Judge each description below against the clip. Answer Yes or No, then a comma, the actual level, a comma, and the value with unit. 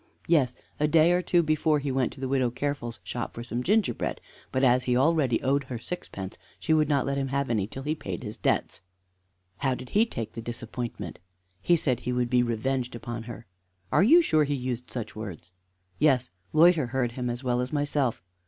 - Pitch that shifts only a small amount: No, average, 3.8 semitones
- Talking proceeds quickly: Yes, fast, 210 wpm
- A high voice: No, low, 130 Hz